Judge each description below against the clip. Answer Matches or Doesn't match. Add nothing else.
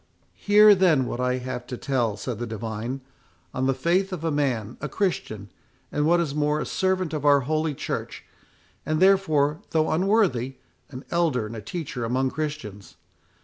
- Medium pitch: Matches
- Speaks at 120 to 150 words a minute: Doesn't match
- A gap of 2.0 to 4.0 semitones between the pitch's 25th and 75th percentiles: Doesn't match